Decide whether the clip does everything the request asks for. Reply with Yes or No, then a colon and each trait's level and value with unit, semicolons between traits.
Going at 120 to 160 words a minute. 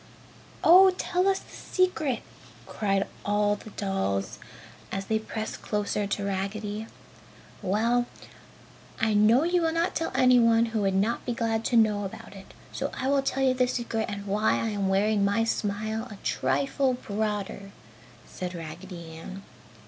Yes: average, 155 wpm